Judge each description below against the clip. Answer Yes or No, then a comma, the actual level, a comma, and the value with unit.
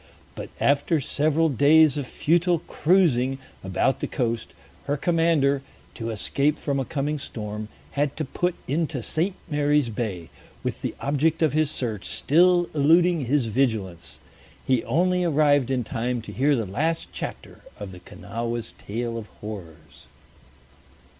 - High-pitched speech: No, medium, 140 Hz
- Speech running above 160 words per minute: No, average, 145 wpm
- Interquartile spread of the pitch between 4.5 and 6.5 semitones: Yes, average, 5.2 semitones